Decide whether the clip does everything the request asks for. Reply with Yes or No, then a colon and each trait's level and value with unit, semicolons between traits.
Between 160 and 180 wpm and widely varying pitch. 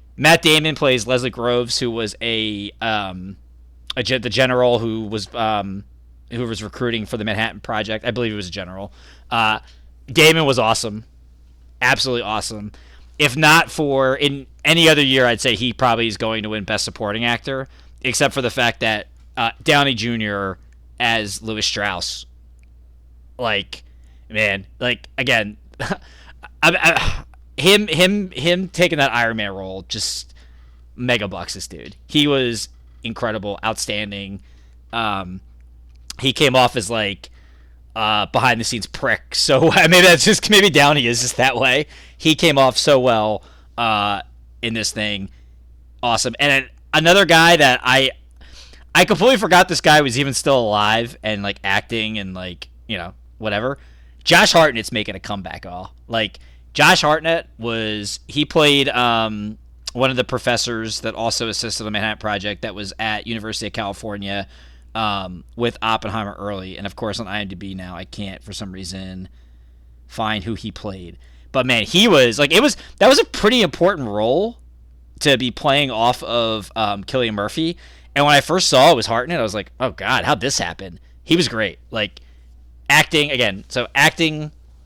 Yes: average, 165 wpm; wide, 5.9 semitones